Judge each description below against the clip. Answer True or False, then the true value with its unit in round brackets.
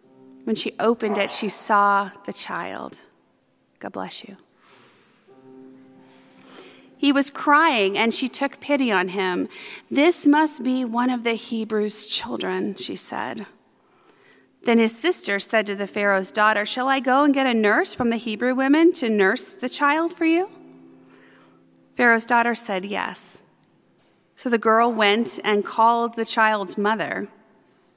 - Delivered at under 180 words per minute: True (145 wpm)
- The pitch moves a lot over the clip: False (4.3 semitones)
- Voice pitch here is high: True (220 Hz)